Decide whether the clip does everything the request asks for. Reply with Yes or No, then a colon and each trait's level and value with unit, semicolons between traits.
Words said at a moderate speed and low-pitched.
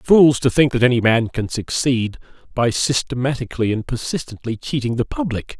Yes: average, 160 wpm; low, 125 Hz